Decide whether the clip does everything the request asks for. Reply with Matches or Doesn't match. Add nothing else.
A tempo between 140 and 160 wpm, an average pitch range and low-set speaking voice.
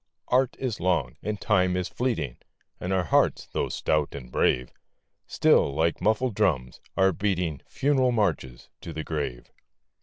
Doesn't match